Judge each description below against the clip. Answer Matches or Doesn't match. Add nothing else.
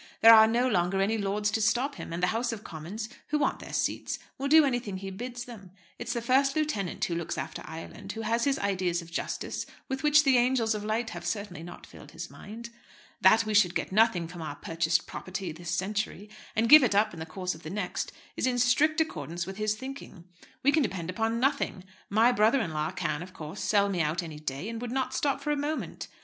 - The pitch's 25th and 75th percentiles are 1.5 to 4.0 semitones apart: Doesn't match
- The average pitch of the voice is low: Doesn't match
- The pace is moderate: Doesn't match